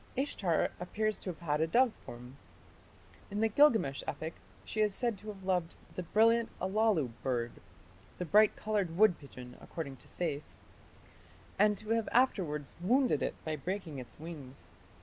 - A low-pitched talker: No, medium, 180 Hz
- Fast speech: No, average, 160 wpm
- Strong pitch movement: Yes, wide, 6.3 semitones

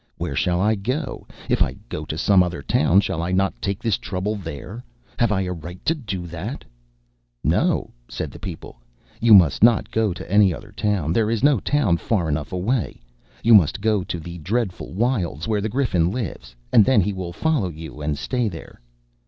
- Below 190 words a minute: No, average, 200 wpm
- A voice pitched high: No, very low, 95 Hz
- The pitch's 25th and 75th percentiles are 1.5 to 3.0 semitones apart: No, average, 4.4 semitones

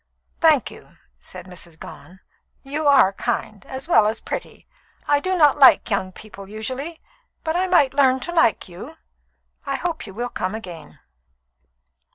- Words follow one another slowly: No, average, 160 wpm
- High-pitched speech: Yes, very high, 260 Hz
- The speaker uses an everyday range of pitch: No, wide, 7.4 semitones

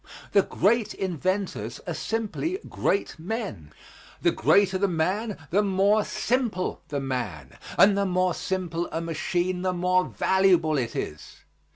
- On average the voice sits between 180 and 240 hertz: Yes, medium, 185 Hz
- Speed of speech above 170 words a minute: No, average, 140 wpm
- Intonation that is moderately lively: Yes, average, 3.6 semitones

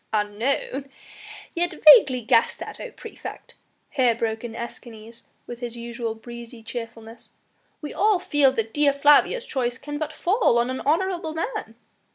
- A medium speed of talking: Yes, average, 150 wpm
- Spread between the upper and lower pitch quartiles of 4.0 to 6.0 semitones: Yes, average, 4.4 semitones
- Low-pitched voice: No, high, 245 Hz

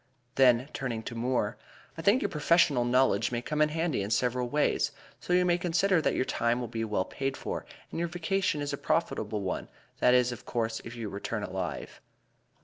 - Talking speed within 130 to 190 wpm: No, average, 200 wpm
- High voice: No, low, 125 Hz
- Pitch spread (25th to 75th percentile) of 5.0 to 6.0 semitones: Yes, wide, 5.6 semitones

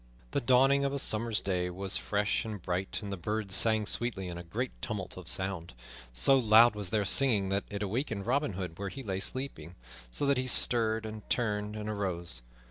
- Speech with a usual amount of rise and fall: Yes, average, 3.8 semitones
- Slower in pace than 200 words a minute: No, fast, 205 wpm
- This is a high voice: No, low, 105 Hz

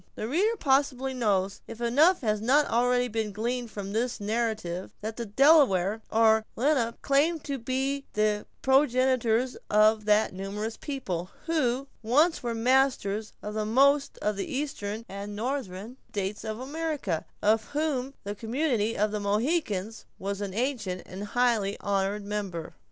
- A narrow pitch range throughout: No, average, 4.4 semitones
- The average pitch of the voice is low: No, high, 225 Hz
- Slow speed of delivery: No, average, 145 wpm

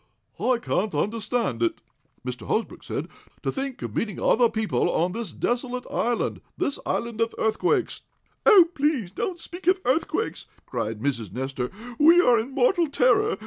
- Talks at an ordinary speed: Yes, average, 155 wpm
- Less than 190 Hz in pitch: No, high, 235 Hz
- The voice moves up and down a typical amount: No, wide, 7.2 semitones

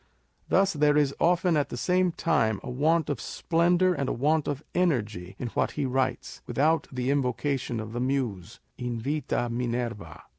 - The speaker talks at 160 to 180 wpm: Yes, average, 175 wpm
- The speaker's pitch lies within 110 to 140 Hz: Yes, low, 135 Hz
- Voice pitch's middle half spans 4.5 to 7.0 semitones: Yes, average, 4.9 semitones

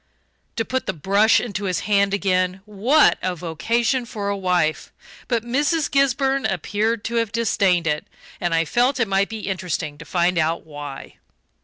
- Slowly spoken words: No, average, 170 wpm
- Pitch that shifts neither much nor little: Yes, average, 4.8 semitones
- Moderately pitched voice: No, high, 200 Hz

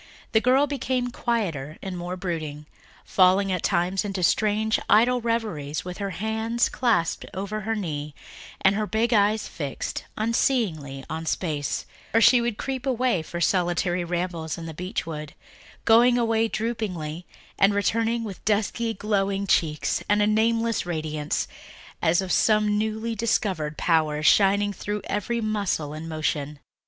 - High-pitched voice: Yes, high, 200 Hz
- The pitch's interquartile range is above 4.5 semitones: Yes, average, 5.2 semitones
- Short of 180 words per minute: Yes, average, 145 wpm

